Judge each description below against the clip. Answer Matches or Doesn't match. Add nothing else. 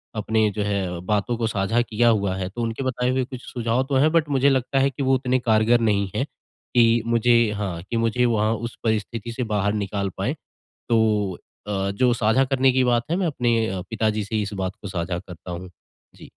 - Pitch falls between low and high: Doesn't match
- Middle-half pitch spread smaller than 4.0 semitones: Matches